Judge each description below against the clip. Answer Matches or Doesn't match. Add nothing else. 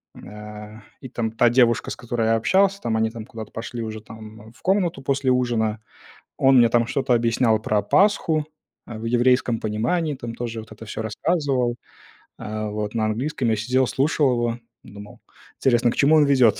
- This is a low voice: Matches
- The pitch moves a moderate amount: Matches